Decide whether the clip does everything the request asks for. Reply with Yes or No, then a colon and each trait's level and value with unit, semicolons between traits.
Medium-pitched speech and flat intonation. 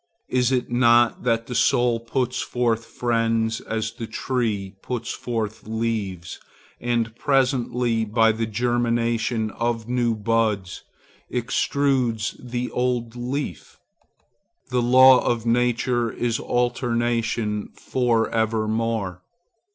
No: low, 115 Hz; narrow, 1.5 semitones